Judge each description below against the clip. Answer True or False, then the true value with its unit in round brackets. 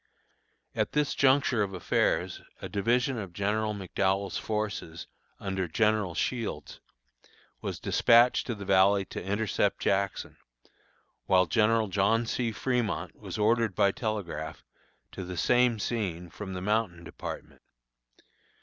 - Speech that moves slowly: True (125 wpm)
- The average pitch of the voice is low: True (105 Hz)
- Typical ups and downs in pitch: True (3.2 semitones)